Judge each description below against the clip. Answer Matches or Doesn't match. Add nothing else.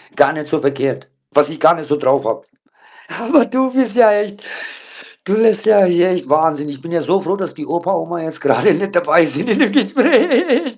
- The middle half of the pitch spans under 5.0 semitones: Doesn't match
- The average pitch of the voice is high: Doesn't match